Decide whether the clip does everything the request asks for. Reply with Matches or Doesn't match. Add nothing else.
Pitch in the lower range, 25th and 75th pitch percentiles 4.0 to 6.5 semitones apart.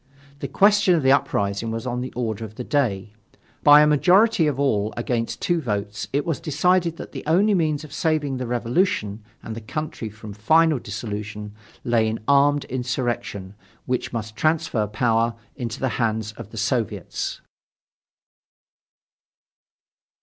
Matches